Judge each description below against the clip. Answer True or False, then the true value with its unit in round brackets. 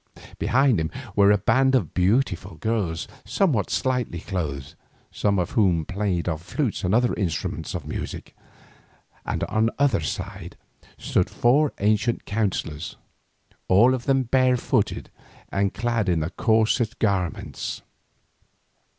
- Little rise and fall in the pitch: False (5.0 semitones)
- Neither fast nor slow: False (125 wpm)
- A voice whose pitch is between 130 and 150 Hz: False (105 Hz)